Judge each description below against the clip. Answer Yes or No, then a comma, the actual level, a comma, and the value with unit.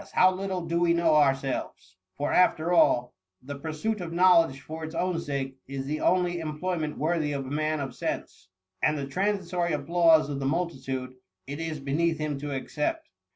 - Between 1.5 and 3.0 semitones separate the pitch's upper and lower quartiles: No, average, 3.9 semitones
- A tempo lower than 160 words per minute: No, average, 180 wpm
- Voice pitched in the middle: Yes, medium, 155 Hz